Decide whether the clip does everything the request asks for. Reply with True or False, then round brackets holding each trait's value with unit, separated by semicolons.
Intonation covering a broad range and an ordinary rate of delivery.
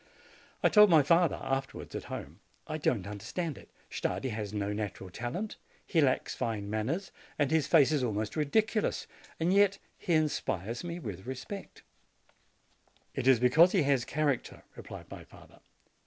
True (7.0 semitones; 155 wpm)